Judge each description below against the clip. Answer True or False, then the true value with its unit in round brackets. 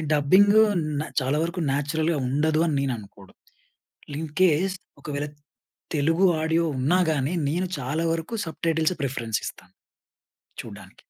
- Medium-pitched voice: True (155 Hz)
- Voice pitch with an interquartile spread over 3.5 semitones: False (3.1 semitones)